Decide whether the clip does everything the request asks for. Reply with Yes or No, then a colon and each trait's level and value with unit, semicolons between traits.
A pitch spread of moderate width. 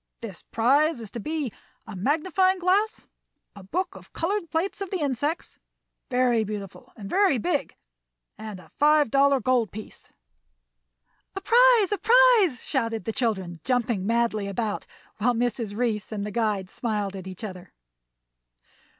No: wide, 7.3 semitones